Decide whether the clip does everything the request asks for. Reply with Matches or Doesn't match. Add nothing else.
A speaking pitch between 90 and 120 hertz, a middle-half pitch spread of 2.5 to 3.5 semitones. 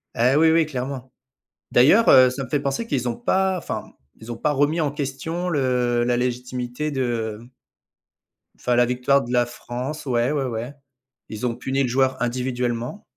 Doesn't match